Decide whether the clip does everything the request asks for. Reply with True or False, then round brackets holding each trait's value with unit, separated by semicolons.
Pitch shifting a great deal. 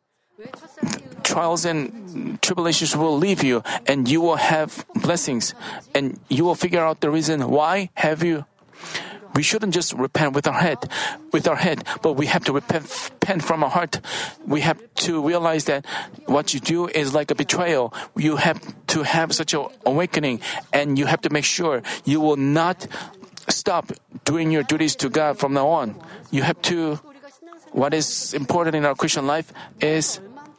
False (2.9 semitones)